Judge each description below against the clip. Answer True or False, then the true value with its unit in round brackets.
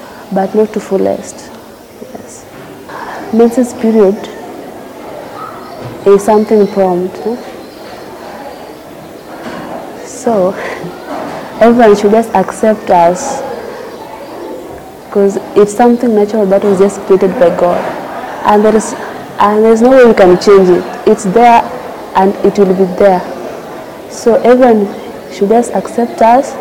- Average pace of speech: False (115 wpm)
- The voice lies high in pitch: True (210 Hz)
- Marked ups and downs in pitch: False (3.0 semitones)